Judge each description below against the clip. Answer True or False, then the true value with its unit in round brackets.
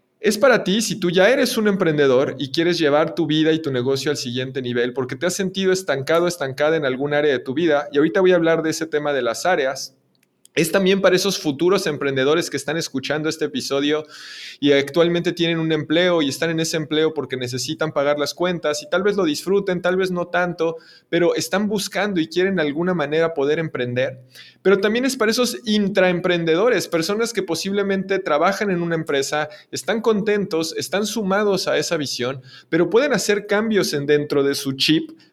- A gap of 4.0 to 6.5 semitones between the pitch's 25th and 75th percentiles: True (4.4 semitones)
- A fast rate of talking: True (200 wpm)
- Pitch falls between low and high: True (165 Hz)